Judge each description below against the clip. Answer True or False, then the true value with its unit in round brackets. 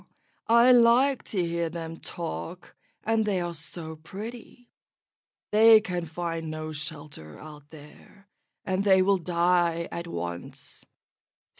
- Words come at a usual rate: False (125 wpm)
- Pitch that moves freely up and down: False (4.3 semitones)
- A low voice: False (175 Hz)